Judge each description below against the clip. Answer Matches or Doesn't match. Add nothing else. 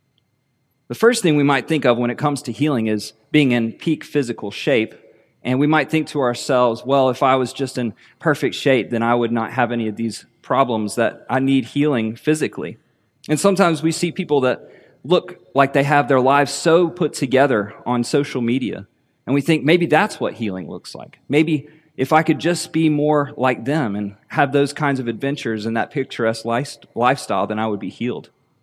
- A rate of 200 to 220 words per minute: Matches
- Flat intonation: Doesn't match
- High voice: Doesn't match